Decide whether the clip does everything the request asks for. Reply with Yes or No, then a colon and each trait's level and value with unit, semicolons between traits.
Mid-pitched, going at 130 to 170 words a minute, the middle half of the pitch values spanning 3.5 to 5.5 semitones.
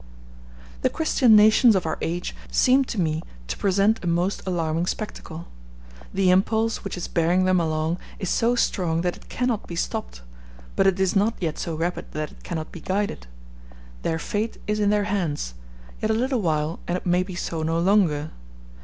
No: medium, 180 Hz; average, 190 wpm; average, 4.2 semitones